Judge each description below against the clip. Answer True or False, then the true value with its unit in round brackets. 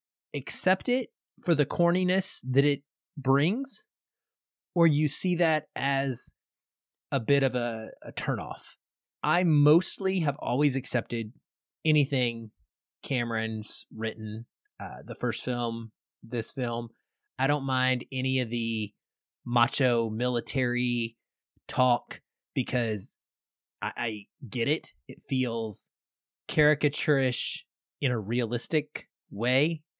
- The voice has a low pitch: True (130 Hz)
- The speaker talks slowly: True (110 wpm)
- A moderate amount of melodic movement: True (4.3 semitones)